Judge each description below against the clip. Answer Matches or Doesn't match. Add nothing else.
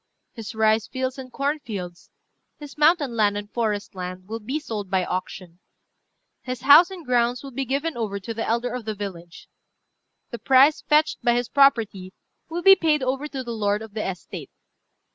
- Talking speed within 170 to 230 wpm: Matches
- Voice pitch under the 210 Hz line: Doesn't match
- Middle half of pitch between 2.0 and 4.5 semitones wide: Doesn't match